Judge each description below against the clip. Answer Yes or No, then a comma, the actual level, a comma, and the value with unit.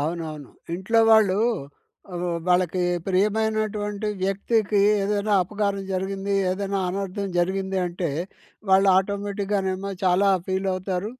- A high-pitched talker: Yes, high, 195 Hz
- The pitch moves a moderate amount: No, narrow, 1.6 semitones